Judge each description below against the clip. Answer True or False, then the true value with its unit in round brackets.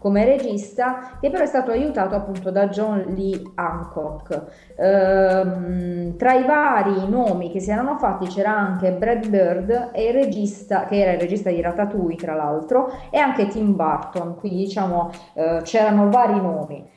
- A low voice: False (195 Hz)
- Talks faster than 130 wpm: True (150 wpm)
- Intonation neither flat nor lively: True (4.2 semitones)